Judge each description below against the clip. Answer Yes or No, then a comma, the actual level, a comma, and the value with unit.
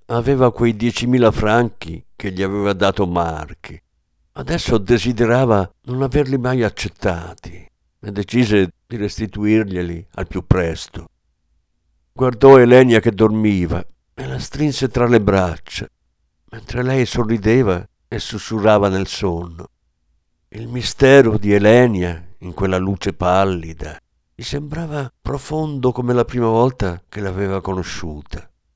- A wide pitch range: Yes, wide, 5.7 semitones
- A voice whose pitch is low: Yes, low, 105 Hz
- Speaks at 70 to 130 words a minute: Yes, average, 120 wpm